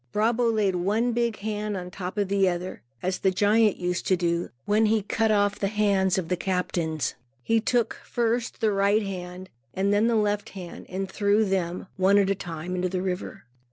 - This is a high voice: Yes, high, 195 Hz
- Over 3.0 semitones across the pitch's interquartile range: No, average, 2.7 semitones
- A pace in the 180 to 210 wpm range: Yes, average, 195 wpm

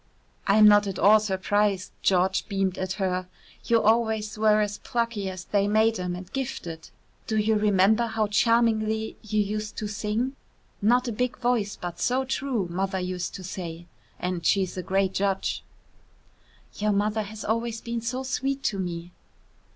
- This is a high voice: Yes, high, 210 Hz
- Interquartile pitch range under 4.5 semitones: Yes, average, 2.8 semitones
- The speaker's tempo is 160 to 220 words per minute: Yes, average, 165 wpm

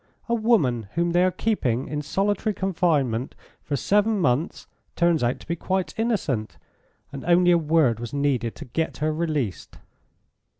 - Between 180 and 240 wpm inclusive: No, average, 160 wpm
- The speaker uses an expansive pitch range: Yes, wide, 6.3 semitones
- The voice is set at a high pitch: No, medium, 160 Hz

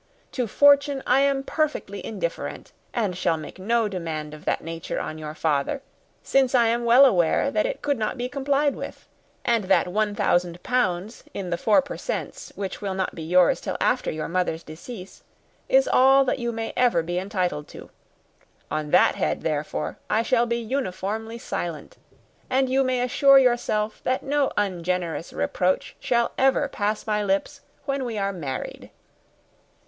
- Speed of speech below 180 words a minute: Yes, average, 170 wpm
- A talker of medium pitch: No, high, 215 Hz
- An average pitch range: No, wide, 6.3 semitones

